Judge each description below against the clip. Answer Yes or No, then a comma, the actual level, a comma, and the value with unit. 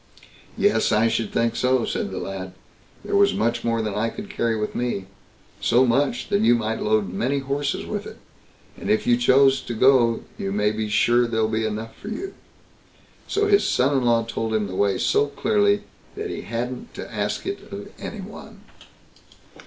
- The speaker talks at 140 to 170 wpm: No, average, 190 wpm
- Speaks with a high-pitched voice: No, low, 120 Hz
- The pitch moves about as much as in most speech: Yes, average, 4.1 semitones